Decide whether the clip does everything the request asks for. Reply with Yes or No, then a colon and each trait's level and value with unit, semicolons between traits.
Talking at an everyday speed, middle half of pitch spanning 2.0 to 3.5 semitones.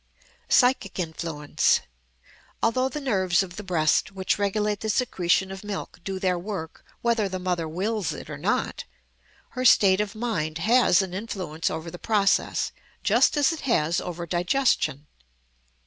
No: average, 150 wpm; average, 4.1 semitones